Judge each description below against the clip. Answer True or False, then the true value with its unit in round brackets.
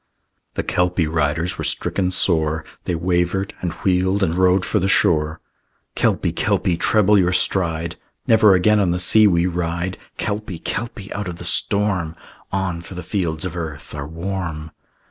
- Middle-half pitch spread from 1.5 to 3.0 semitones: True (2.6 semitones)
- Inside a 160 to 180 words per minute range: True (165 wpm)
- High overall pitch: False (90 Hz)